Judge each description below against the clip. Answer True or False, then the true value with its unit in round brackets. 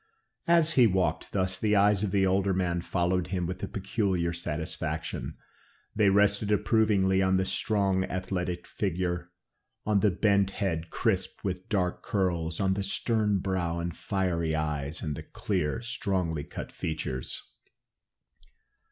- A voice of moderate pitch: False (95 Hz)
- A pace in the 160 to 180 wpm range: False (145 wpm)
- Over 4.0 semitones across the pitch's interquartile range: False (2.6 semitones)